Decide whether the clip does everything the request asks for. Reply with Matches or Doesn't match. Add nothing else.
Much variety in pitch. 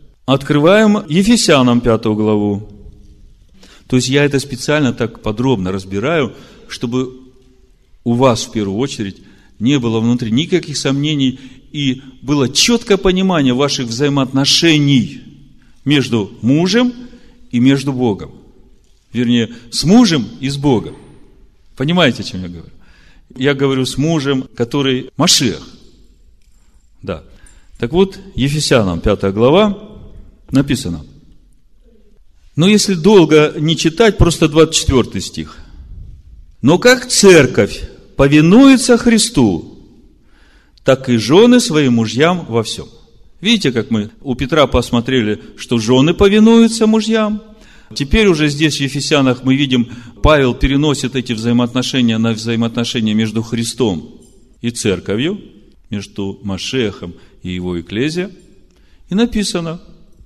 Matches